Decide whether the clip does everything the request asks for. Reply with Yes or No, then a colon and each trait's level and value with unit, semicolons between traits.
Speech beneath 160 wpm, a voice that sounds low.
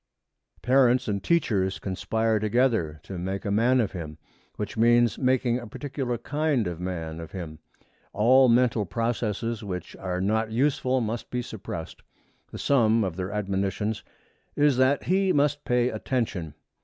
Yes: average, 150 wpm; low, 110 Hz